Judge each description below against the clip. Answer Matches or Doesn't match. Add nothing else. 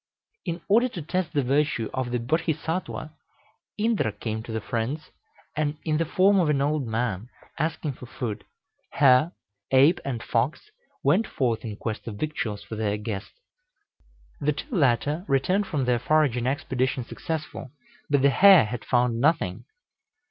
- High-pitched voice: Doesn't match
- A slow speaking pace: Doesn't match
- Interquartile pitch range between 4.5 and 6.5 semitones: Matches